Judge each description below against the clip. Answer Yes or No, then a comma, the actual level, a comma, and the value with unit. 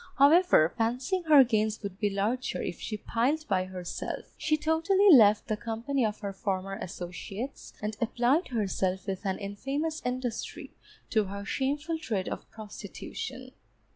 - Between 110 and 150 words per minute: Yes, average, 145 wpm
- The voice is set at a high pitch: Yes, high, 225 Hz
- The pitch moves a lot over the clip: Yes, wide, 5.7 semitones